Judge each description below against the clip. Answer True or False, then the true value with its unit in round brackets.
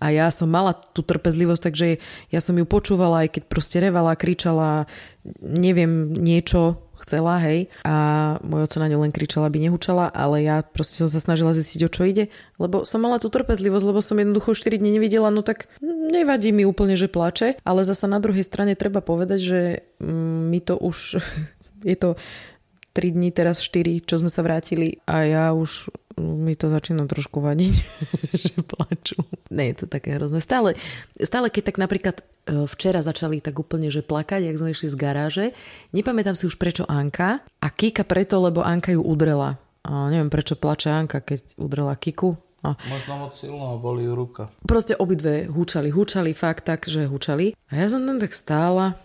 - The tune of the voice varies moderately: True (3.5 semitones)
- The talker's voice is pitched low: False (170 Hz)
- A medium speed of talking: False (180 wpm)